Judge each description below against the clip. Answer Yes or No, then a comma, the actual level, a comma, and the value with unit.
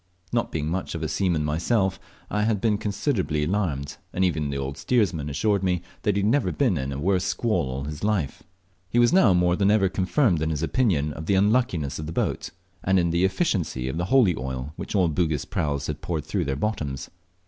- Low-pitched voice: Yes, very low, 90 Hz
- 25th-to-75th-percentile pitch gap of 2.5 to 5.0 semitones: No, wide, 5.4 semitones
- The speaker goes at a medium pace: No, fast, 215 wpm